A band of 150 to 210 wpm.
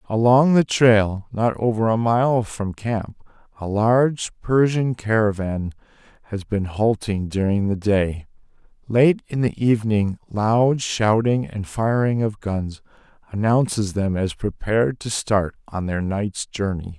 No: average, 140 wpm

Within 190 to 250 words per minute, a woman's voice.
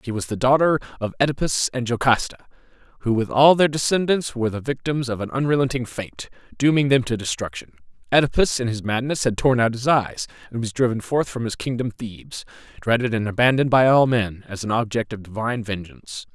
No: average, 195 wpm; male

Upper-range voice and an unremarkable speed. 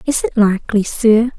Yes: high, 220 Hz; average, 175 wpm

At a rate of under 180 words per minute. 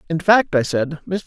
No: fast, 240 wpm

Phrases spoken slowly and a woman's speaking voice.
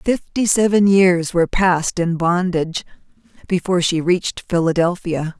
Yes: slow, 120 wpm; female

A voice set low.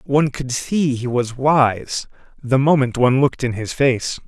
Yes: low, 130 Hz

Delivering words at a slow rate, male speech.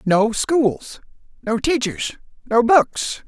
Yes: slow, 110 wpm; male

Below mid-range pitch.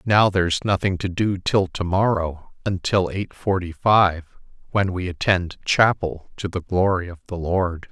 Yes: very low, 95 Hz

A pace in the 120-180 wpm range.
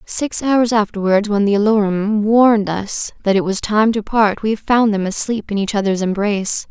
No: average, 195 wpm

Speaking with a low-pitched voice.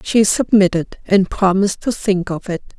No: high, 195 Hz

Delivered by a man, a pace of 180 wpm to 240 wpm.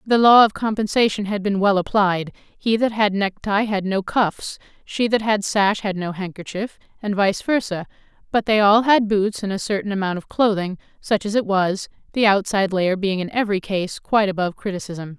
No: female; average, 200 wpm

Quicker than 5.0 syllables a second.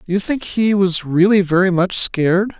No: 4.9 syllables/s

